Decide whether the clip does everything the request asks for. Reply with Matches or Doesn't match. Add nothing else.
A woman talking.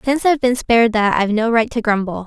Matches